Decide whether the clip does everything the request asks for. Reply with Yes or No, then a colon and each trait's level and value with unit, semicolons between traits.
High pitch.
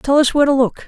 Yes: very high, 270 Hz